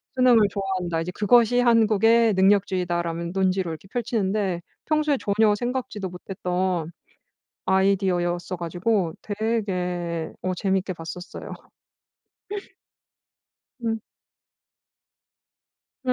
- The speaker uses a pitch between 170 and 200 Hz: Yes, high, 190 Hz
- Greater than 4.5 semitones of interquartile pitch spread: No, average, 3.7 semitones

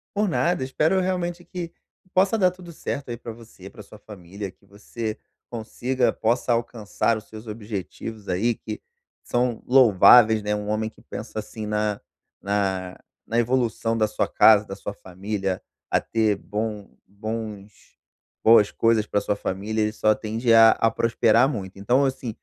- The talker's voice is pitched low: Yes, low, 110 Hz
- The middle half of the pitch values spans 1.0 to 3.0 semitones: Yes, narrow, 2.6 semitones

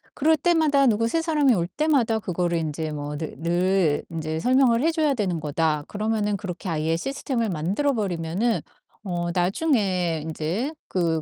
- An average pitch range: No, wide, 7.6 semitones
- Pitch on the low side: No, high, 190 Hz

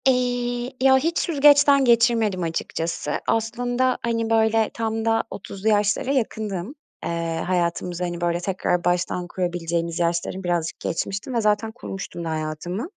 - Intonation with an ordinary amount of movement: No, wide, 5.7 semitones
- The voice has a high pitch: Yes, high, 210 Hz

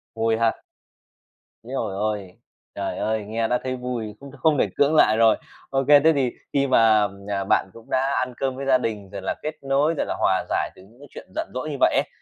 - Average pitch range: Yes, average, 4.0 semitones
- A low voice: Yes, low, 125 Hz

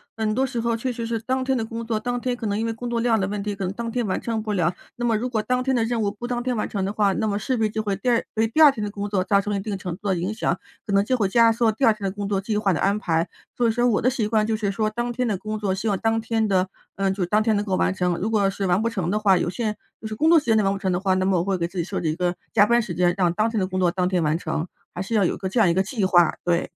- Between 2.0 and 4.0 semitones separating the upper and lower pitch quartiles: Yes, average, 3.2 semitones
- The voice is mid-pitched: No, high, 210 Hz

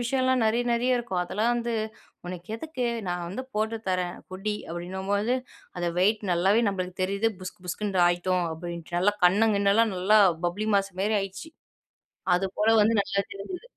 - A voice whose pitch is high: Yes, high, 200 Hz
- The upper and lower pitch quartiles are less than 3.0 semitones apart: No, average, 3.7 semitones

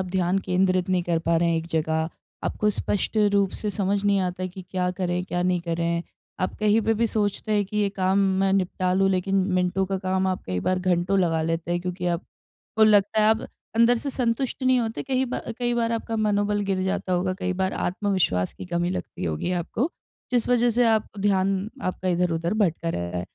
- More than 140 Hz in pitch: Yes, medium, 185 Hz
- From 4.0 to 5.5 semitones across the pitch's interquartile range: No, average, 3.0 semitones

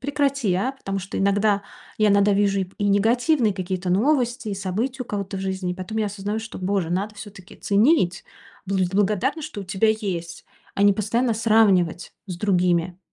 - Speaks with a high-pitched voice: Yes, high, 200 Hz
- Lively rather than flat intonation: No, average, 2.9 semitones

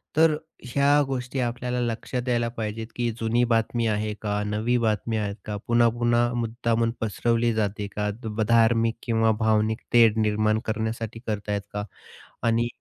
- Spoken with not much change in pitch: Yes, narrow, 1.7 semitones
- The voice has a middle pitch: No, low, 115 Hz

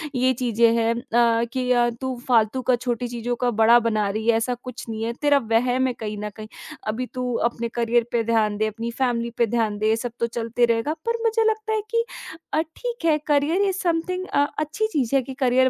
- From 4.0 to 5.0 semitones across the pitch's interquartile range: No, average, 3.6 semitones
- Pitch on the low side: No, high, 245 Hz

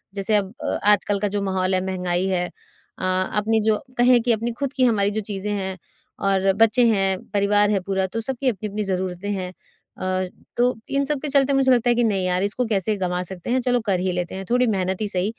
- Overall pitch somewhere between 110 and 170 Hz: No, high, 200 Hz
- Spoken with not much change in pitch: No, average, 3.7 semitones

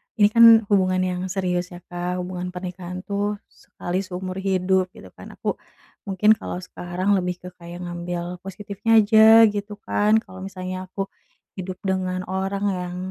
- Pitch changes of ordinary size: No, narrow, 1.8 semitones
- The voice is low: No, medium, 185 Hz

